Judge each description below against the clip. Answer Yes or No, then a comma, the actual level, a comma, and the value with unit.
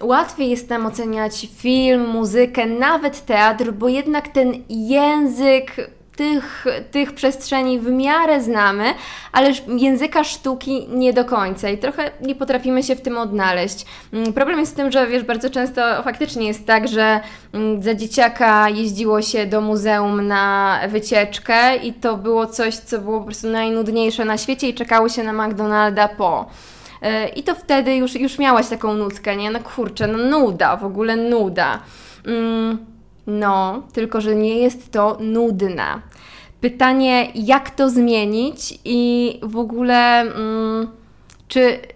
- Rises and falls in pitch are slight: No, average, 3.1 semitones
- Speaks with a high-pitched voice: Yes, high, 235 Hz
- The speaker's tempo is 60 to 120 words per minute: No, average, 145 wpm